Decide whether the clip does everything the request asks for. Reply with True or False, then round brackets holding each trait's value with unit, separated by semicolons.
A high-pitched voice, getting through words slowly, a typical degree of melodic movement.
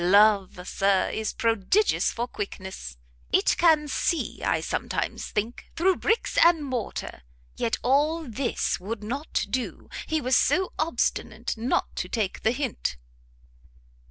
False (240 Hz; 130 wpm; 6.3 semitones)